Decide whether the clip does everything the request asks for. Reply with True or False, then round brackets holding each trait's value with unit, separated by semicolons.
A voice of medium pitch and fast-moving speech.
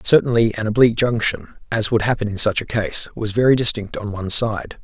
False (110 Hz; 210 wpm)